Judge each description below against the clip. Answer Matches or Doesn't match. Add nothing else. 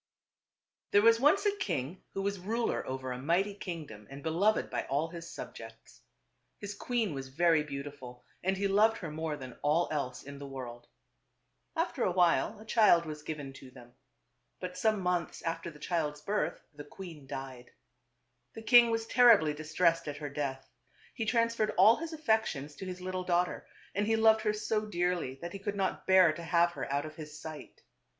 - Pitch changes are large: Matches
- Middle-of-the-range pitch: Matches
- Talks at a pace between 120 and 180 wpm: Doesn't match